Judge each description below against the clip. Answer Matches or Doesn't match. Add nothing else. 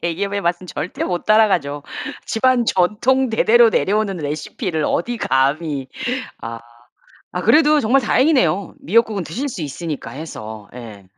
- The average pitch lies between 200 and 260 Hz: Doesn't match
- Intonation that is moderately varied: Doesn't match